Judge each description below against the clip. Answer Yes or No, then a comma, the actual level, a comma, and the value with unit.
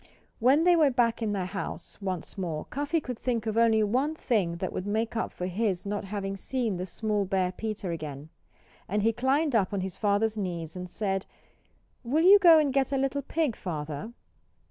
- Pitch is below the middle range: No, high, 215 Hz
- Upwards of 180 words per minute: Yes, average, 200 wpm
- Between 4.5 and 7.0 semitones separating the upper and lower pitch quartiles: Yes, wide, 5.5 semitones